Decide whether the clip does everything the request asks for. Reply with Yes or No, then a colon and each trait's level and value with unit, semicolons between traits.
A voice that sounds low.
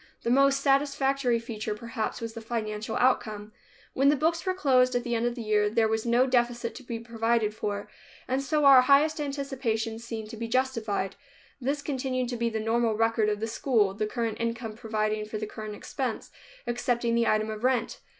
No: high, 235 Hz